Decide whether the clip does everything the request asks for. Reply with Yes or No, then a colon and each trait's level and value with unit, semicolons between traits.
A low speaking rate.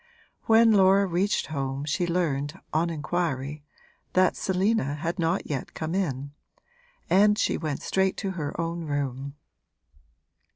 Yes: slow, 130 wpm